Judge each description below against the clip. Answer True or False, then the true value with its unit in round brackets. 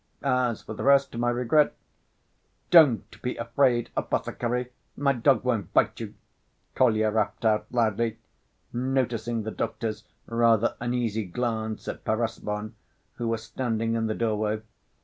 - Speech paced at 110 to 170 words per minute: True (135 wpm)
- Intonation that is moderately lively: False (2.0 semitones)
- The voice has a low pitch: True (115 Hz)